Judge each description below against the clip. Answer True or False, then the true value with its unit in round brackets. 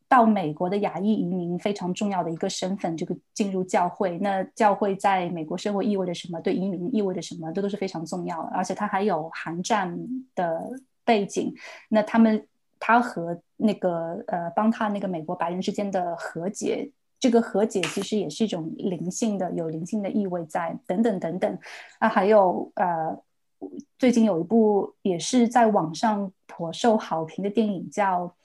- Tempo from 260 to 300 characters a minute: True (275 characters per minute)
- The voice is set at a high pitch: True (195 Hz)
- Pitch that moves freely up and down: False (3.5 semitones)